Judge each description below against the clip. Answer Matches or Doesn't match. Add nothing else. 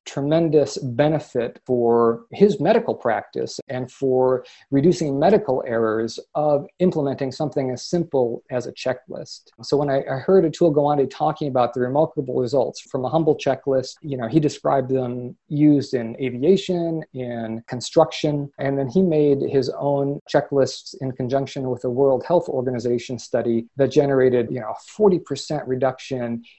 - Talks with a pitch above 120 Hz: Matches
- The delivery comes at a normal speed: Matches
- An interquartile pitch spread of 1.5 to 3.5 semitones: Matches